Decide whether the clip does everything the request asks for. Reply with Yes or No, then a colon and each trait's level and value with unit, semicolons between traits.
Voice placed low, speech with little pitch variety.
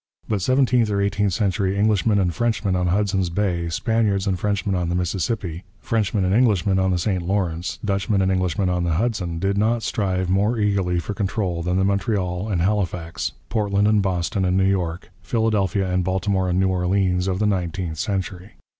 Yes: very low, 95 Hz; narrow, 2.3 semitones